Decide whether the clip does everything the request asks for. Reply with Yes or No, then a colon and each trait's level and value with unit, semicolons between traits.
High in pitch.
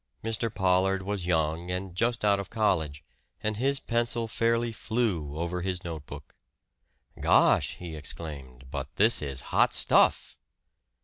No: very low, 90 Hz